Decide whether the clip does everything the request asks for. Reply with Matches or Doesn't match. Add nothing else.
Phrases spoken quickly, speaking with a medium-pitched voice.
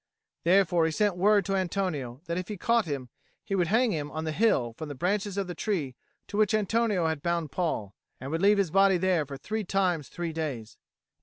Matches